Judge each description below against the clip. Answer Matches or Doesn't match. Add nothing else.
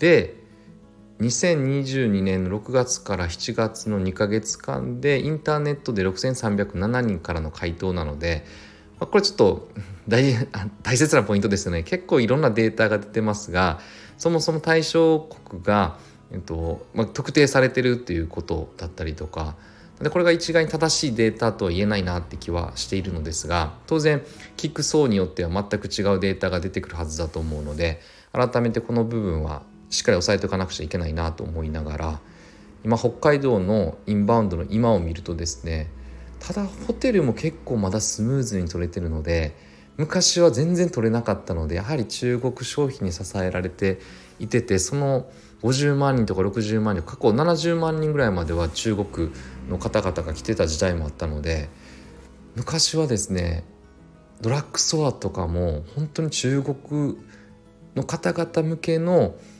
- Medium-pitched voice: Doesn't match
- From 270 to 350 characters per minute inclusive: Matches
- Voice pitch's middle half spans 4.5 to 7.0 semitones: Doesn't match